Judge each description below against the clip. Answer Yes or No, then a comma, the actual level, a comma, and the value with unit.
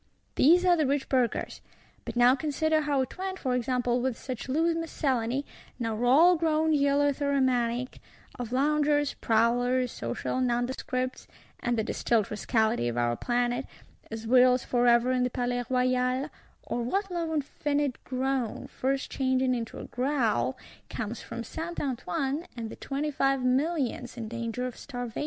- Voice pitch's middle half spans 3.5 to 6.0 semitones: No, average, 3.0 semitones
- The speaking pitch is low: No, very high, 255 Hz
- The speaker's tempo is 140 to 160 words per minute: Yes, average, 145 wpm